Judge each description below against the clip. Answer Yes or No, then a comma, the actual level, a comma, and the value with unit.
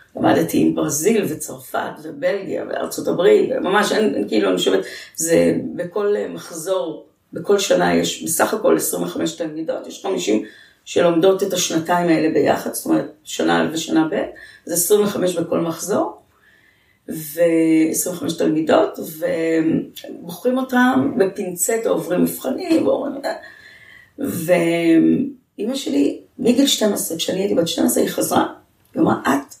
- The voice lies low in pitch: No, medium, 180 Hz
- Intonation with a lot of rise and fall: Yes, wide, 6.2 semitones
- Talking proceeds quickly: No, average, 120 wpm